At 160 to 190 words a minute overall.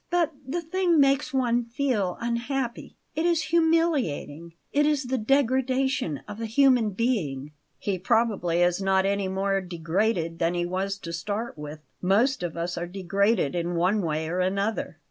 Yes: average, 165 wpm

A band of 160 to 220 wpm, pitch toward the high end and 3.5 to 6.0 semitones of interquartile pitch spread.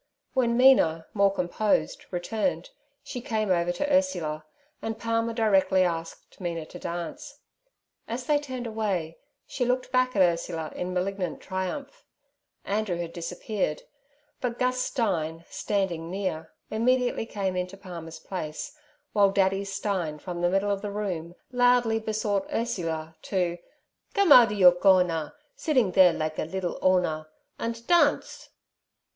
No: average, 140 wpm; high, 195 Hz; average, 4.9 semitones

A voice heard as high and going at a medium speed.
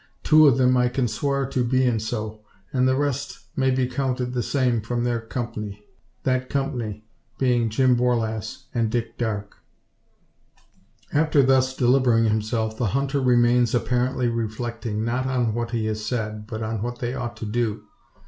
No: low, 120 Hz; average, 160 wpm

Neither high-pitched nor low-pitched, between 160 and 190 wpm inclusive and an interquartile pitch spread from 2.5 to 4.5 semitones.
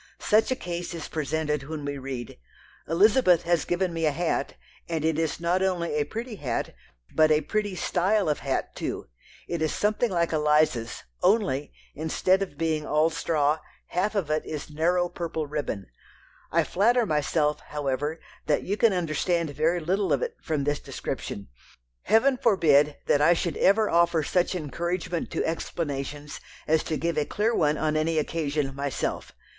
Yes: medium, 160 Hz; average, 170 wpm; average, 3.2 semitones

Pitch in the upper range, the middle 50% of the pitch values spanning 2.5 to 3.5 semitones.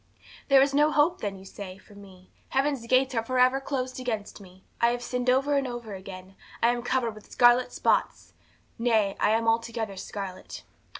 No: high, 235 Hz; average, 4.1 semitones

